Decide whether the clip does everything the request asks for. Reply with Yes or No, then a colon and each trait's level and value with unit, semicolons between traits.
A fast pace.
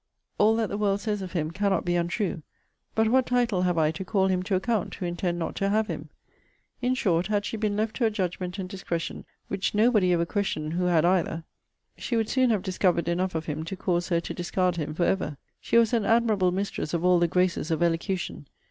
Yes: fast, 230 wpm